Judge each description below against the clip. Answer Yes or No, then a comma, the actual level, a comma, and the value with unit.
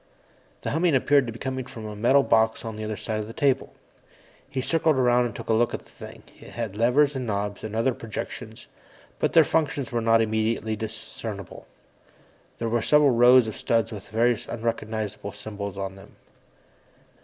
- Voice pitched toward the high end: No, low, 115 Hz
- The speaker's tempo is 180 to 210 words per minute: Yes, average, 190 wpm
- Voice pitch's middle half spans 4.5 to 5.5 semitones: No, average, 2.8 semitones